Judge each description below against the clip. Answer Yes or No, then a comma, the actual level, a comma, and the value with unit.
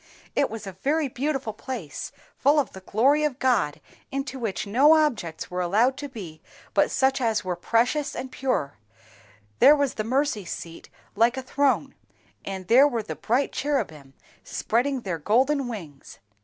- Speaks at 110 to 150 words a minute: No, average, 165 wpm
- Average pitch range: No, wide, 6.0 semitones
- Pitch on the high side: Yes, high, 240 Hz